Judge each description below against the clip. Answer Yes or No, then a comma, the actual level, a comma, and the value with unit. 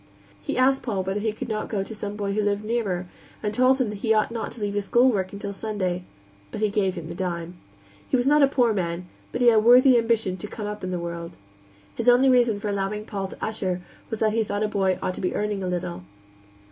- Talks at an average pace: No, fast, 255 wpm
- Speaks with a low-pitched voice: No, high, 210 Hz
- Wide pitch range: No, average, 3.2 semitones